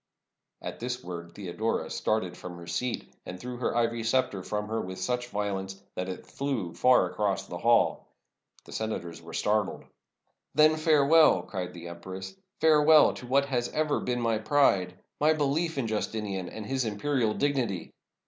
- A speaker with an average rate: Yes, average, 170 wpm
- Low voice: Yes, low, 110 Hz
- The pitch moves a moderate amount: No, wide, 6.4 semitones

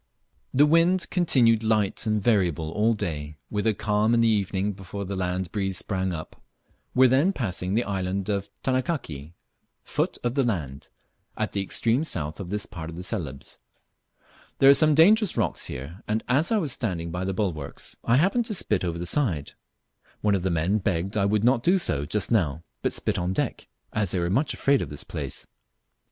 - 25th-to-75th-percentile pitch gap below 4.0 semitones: No, wide, 5.5 semitones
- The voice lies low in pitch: Yes, low, 100 Hz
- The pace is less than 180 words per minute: No, average, 195 wpm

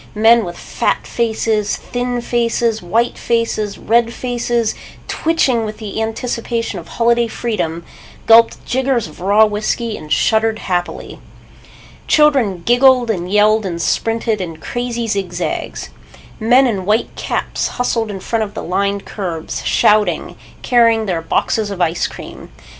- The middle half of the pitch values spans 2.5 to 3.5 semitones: Yes, average, 2.9 semitones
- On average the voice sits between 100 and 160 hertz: No, high, 220 Hz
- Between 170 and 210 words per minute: No, average, 140 wpm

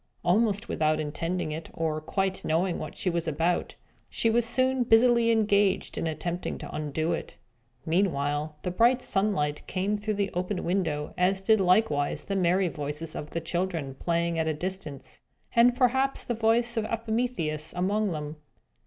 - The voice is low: No, medium, 180 Hz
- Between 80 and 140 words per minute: No, average, 160 wpm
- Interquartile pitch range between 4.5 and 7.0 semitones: Yes, wide, 5.5 semitones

